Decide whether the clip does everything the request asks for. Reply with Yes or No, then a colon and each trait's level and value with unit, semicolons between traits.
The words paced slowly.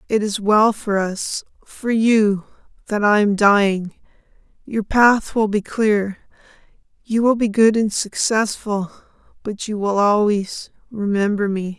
Yes: slow, 110 wpm